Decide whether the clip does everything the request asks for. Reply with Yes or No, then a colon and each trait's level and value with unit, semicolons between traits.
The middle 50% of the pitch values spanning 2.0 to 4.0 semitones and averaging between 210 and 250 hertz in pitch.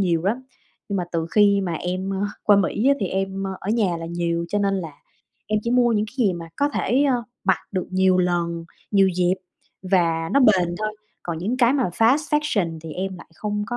No: average, 3.6 semitones; high, 195 Hz